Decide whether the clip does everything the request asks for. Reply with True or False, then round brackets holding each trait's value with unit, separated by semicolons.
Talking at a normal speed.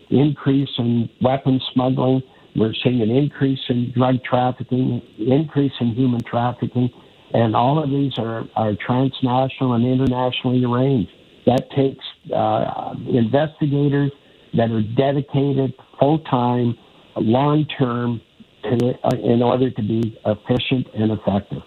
False (120 wpm)